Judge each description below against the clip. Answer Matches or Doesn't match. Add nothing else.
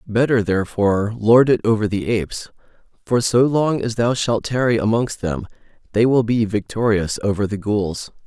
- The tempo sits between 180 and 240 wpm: Doesn't match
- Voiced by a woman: Doesn't match